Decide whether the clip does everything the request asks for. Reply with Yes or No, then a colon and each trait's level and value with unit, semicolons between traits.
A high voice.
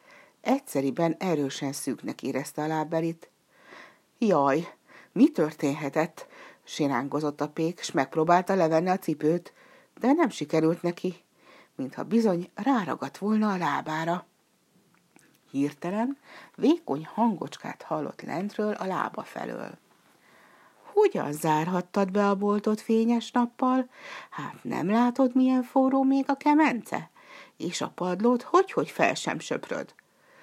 Yes: high, 200 Hz